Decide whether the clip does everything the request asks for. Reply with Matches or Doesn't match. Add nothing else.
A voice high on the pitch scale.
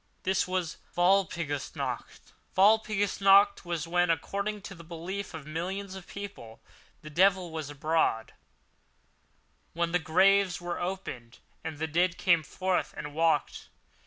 Doesn't match